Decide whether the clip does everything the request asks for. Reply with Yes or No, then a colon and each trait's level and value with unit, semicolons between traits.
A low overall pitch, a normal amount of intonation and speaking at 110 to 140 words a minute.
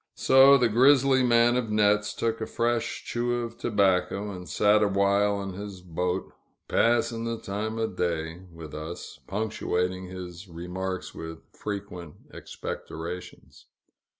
Yes: low, 100 Hz; average, 4.2 semitones; slow, 135 wpm